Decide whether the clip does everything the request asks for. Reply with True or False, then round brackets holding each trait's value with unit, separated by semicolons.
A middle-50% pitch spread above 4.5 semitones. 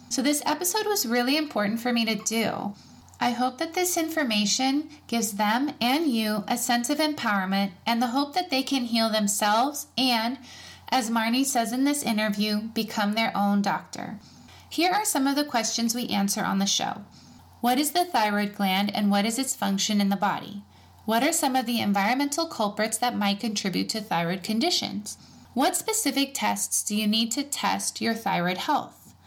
True (4.9 semitones)